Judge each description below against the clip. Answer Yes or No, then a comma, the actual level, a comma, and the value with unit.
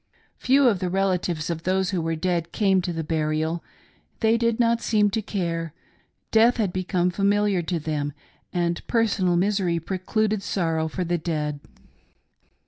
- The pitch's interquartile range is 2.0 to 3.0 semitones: No, average, 3.8 semitones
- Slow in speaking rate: No, average, 165 wpm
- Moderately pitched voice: Yes, medium, 180 Hz